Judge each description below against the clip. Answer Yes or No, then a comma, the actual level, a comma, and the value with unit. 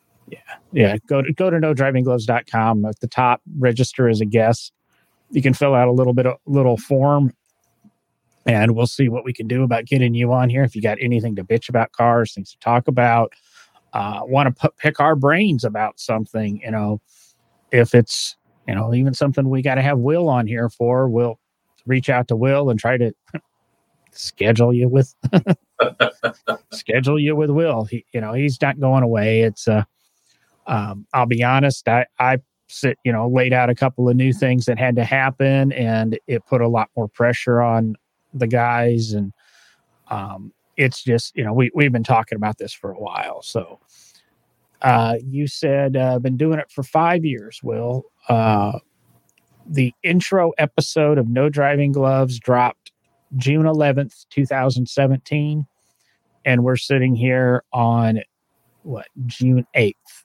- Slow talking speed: No, average, 175 wpm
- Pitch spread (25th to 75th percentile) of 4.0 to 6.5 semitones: No, average, 2.8 semitones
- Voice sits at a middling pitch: No, low, 125 Hz